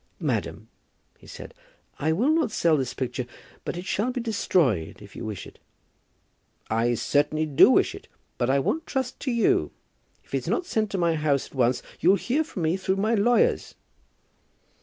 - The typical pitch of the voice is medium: Yes, medium, 175 Hz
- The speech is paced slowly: No, average, 180 wpm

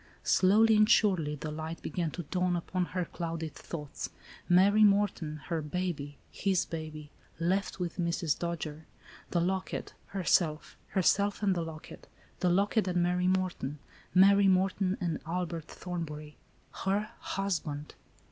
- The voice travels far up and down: No, average, 3.2 semitones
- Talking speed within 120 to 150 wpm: Yes, average, 140 wpm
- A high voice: No, medium, 175 Hz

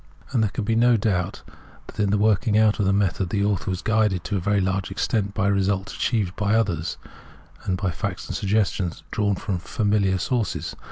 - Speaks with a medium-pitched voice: No, low, 100 Hz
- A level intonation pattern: Yes, narrow, 2.1 semitones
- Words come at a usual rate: No, fast, 210 wpm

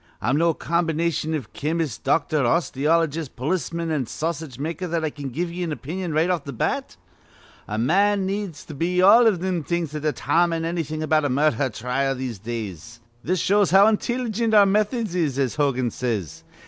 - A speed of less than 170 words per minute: No, average, 185 wpm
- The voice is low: No, medium, 160 Hz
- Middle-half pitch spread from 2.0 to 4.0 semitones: No, average, 4.5 semitones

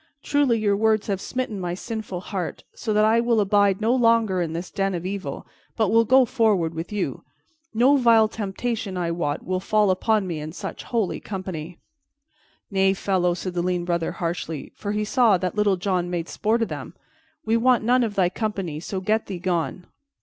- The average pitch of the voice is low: No, high, 200 Hz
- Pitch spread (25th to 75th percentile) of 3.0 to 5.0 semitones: Yes, average, 3.7 semitones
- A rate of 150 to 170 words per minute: No, average, 195 wpm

